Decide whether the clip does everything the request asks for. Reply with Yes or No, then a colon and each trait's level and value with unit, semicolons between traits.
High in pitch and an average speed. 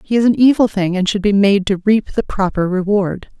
No: high, 200 Hz; fast, 245 wpm